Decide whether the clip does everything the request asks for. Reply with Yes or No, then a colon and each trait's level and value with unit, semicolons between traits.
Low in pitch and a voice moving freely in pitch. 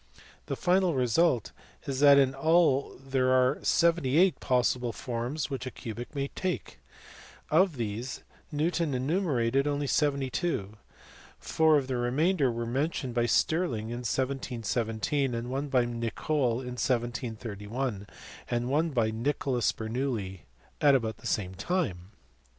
No: low, 130 Hz; average, 3.7 semitones